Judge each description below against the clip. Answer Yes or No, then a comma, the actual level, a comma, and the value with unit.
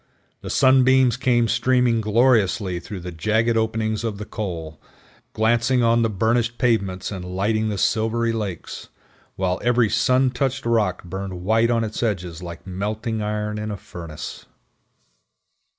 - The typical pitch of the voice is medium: No, low, 110 Hz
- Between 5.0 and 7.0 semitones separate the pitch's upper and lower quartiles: No, average, 3.4 semitones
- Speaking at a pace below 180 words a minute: Yes, average, 145 wpm